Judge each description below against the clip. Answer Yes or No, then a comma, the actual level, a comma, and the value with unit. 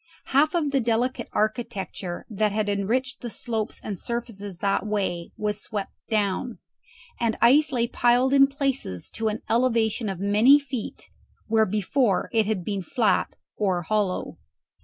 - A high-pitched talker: Yes, high, 220 Hz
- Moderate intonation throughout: Yes, average, 3.6 semitones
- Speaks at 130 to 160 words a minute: Yes, average, 150 wpm